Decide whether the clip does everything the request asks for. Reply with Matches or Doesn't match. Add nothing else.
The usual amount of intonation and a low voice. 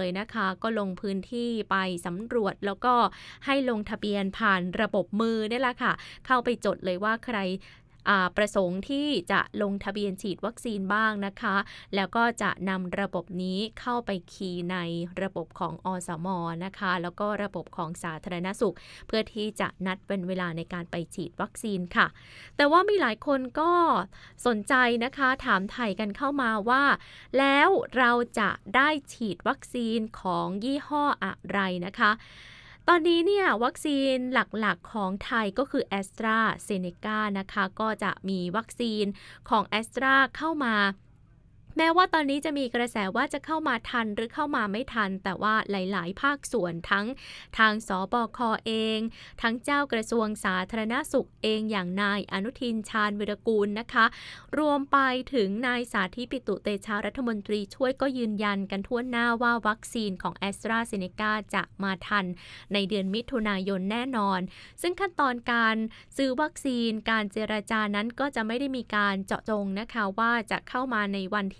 Doesn't match